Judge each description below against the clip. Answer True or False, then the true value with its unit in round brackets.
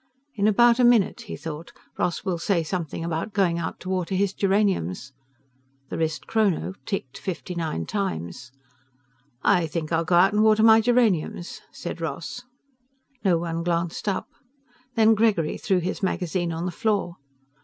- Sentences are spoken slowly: False (155 wpm)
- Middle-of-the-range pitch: True (180 Hz)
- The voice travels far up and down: False (3.9 semitones)